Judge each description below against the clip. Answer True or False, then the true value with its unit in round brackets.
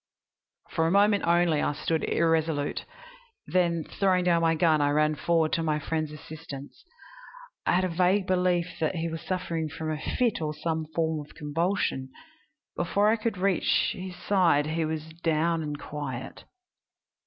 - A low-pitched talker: False (165 Hz)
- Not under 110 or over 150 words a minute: False (165 wpm)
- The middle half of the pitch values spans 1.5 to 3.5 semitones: True (2.8 semitones)